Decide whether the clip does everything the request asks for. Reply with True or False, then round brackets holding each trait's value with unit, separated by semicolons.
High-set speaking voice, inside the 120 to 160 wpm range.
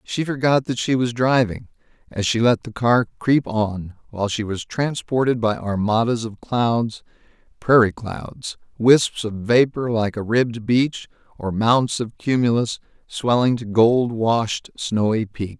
False (115 Hz; 155 wpm)